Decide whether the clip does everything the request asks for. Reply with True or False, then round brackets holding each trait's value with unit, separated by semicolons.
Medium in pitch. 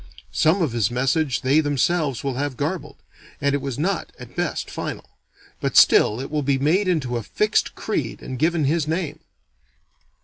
True (145 Hz)